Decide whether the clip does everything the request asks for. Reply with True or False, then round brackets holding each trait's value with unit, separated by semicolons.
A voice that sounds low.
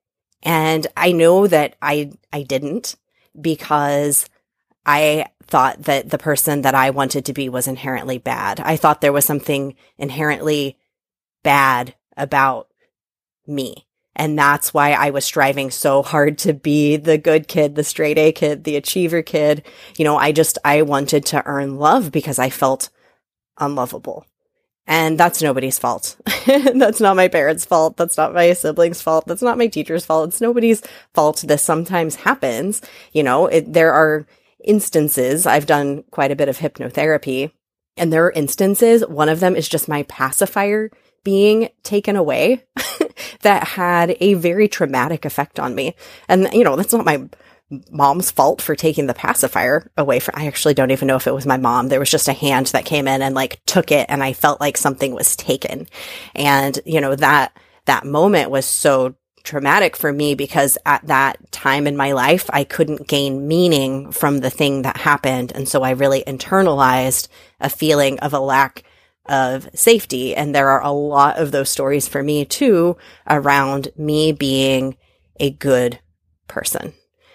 False (150 Hz)